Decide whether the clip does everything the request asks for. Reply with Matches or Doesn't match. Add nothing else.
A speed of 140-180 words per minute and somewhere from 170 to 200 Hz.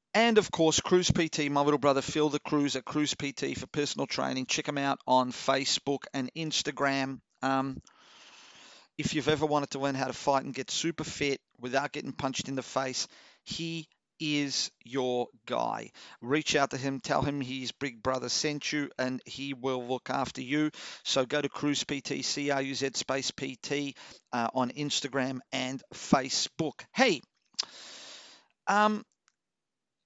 Doesn't match